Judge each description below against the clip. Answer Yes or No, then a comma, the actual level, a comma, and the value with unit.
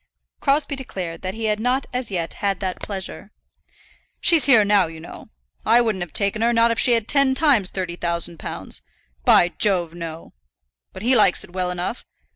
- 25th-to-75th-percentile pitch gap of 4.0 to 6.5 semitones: Yes, average, 5.1 semitones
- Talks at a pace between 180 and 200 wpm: Yes, average, 190 wpm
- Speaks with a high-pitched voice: Yes, high, 205 Hz